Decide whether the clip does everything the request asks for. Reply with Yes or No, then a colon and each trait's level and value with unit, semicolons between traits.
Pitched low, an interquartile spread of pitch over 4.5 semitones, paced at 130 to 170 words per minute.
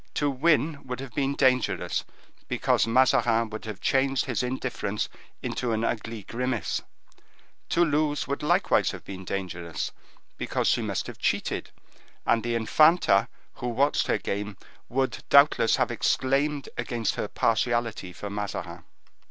No: low, 120 Hz; average, 4.1 semitones; average, 140 wpm